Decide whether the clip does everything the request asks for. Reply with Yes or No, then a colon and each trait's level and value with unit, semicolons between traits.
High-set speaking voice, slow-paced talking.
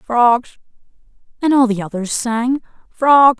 Yes: high, 245 Hz; slow, 125 wpm